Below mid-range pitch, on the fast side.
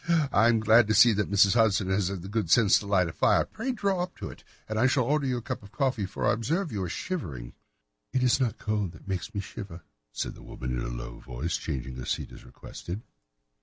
Yes: low, 105 Hz; fast, 265 wpm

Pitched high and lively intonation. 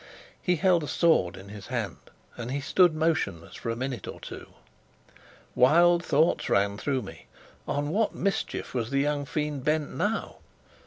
No: medium, 145 Hz; wide, 6.0 semitones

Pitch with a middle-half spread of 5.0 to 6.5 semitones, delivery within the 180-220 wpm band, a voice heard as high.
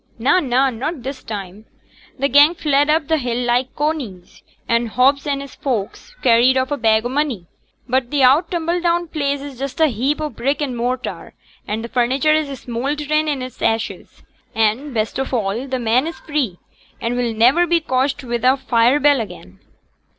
No: average, 3.7 semitones; average, 185 wpm; very high, 260 Hz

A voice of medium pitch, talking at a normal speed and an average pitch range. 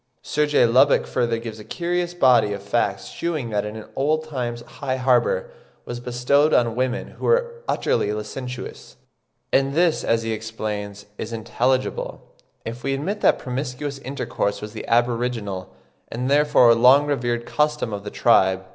No: low, 125 Hz; average, 155 wpm; average, 4.1 semitones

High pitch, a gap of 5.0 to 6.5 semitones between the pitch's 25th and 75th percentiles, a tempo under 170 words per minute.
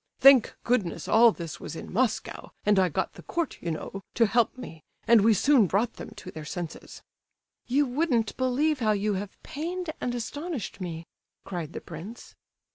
No: high, 225 Hz; wide, 5.6 semitones; average, 180 wpm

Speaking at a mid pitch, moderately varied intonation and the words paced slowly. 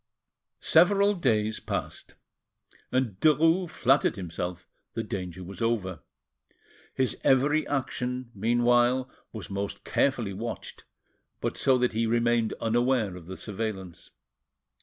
No: low, 115 Hz; average, 4.7 semitones; slow, 120 wpm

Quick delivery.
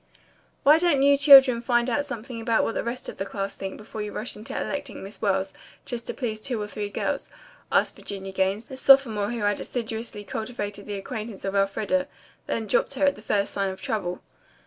Yes: fast, 210 wpm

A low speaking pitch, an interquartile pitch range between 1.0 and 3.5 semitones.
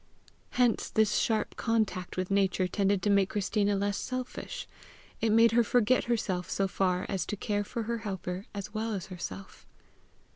No: high, 205 Hz; average, 2.8 semitones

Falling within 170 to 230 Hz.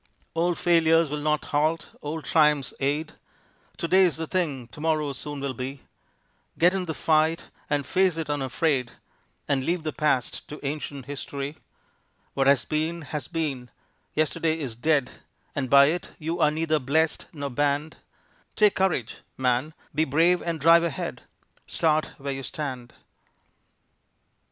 No: medium, 150 Hz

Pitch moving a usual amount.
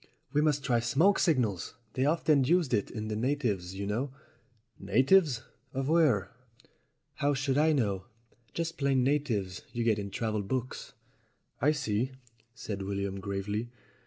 No: wide, 5.9 semitones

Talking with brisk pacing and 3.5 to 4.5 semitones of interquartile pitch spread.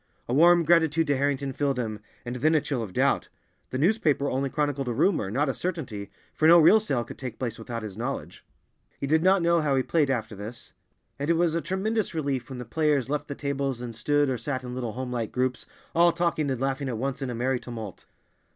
Yes: fast, 235 wpm; average, 4.2 semitones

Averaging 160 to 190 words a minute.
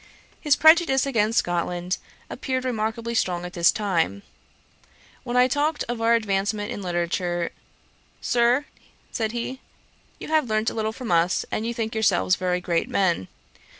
No: average, 150 wpm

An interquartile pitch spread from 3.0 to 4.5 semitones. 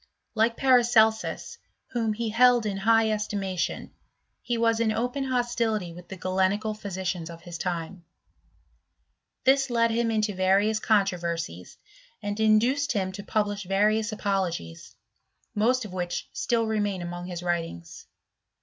Yes: average, 3.7 semitones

